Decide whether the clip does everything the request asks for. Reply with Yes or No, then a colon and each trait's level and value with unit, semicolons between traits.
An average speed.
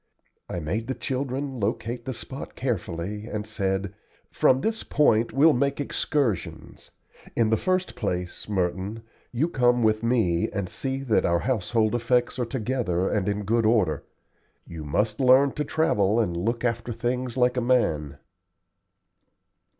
Yes: average, 150 wpm